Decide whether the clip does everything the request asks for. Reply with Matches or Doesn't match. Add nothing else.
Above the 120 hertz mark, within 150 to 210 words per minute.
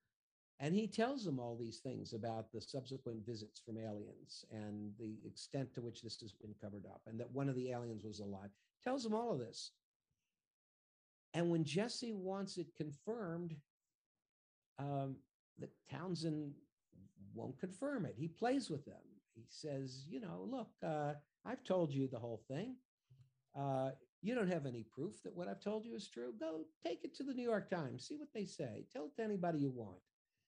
Matches